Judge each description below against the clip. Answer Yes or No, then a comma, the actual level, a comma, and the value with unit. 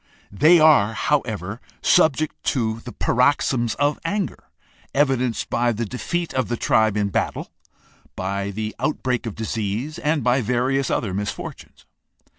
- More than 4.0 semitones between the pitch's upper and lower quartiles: Yes, average, 4.8 semitones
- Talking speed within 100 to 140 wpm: Yes, slow, 135 wpm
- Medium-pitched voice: No, low, 120 Hz